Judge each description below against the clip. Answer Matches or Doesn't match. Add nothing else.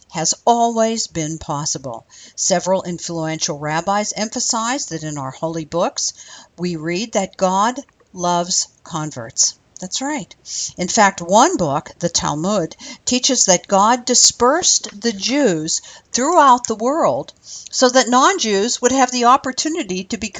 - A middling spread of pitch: Doesn't match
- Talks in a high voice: Matches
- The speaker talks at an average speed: Doesn't match